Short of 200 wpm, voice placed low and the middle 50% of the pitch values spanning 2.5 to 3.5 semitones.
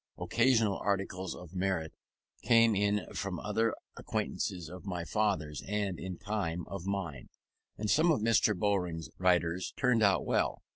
Yes: average, 145 wpm; low, 100 Hz; average, 3.1 semitones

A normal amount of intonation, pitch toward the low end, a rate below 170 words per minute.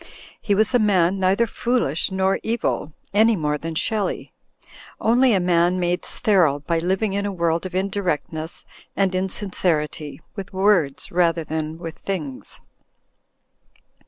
No: average, 3.6 semitones; medium, 185 Hz; average, 140 wpm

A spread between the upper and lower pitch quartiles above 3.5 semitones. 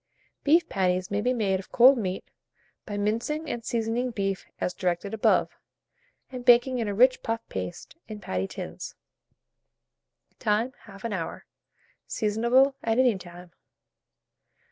Yes: average, 4.1 semitones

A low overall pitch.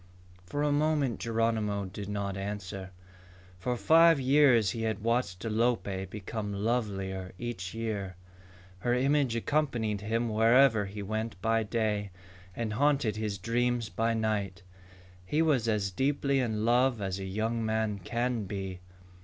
Yes: low, 110 Hz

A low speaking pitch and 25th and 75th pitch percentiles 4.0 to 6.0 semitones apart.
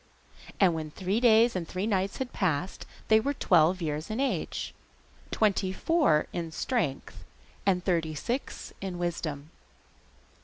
No: medium, 185 Hz; average, 5.2 semitones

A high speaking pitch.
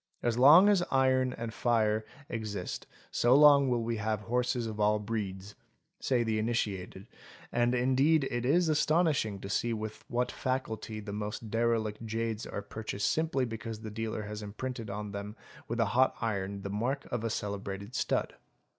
No: low, 115 Hz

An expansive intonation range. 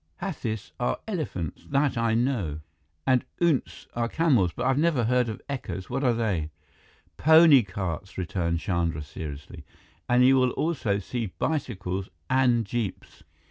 Yes: wide, 6.0 semitones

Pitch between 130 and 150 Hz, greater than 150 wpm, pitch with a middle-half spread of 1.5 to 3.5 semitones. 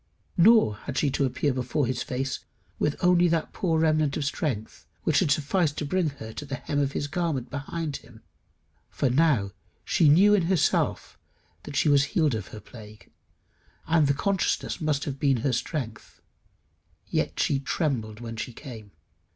No: medium, 140 Hz; average, 170 wpm; average, 4.2 semitones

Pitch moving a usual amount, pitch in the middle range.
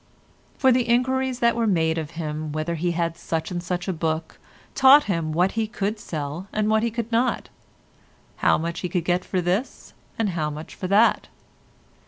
No: wide, 5.7 semitones; medium, 180 Hz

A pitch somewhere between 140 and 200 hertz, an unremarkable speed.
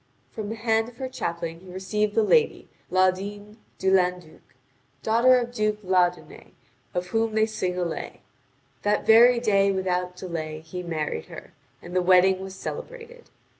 Yes: high, 190 Hz; average, 160 wpm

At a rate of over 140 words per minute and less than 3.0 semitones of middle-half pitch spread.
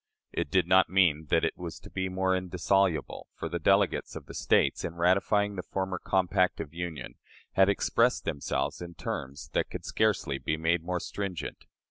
Yes: average, 180 wpm; narrow, 2.6 semitones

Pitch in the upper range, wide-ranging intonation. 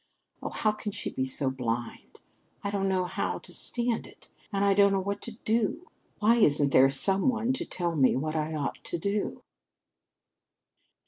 Yes: high, 195 Hz; wide, 6.3 semitones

